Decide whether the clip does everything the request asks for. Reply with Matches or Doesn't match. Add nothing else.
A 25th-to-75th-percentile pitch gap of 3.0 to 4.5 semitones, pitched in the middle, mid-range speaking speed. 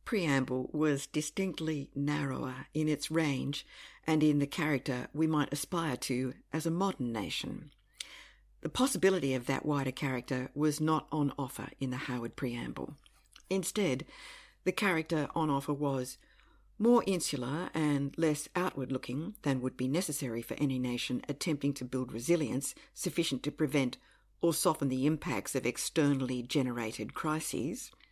Matches